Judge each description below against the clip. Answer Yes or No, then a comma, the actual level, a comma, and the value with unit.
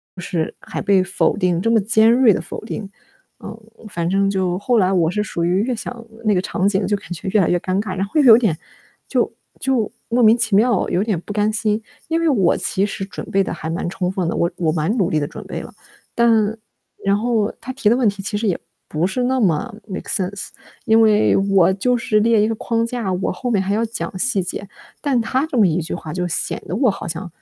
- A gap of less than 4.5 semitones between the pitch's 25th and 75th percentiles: Yes, average, 3.7 semitones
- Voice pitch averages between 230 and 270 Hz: No, high, 205 Hz